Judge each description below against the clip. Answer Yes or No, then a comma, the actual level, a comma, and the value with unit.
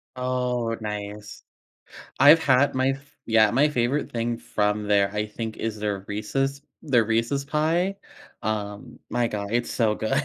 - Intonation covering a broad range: No, average, 4.3 semitones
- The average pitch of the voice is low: Yes, low, 115 Hz